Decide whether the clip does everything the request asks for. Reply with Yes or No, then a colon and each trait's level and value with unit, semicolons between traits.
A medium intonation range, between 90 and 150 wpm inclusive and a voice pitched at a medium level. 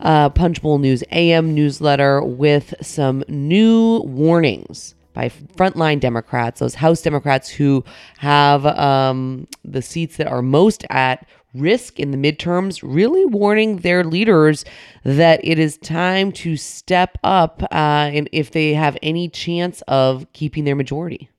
Yes: average, 3.3 semitones; average, 145 wpm; medium, 155 Hz